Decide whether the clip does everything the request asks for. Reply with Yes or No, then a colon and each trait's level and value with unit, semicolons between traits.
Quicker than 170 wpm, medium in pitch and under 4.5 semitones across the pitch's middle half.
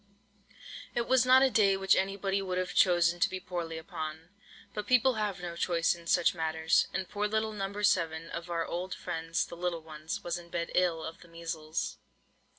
Yes: average, 195 wpm; medium, 175 Hz; average, 3.0 semitones